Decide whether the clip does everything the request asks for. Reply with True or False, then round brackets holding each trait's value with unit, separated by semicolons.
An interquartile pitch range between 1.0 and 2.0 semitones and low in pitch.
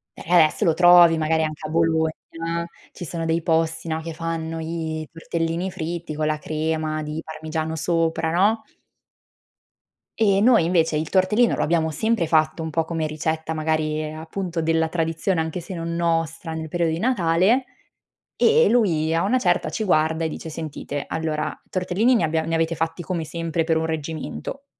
False (1.6 semitones; 165 Hz)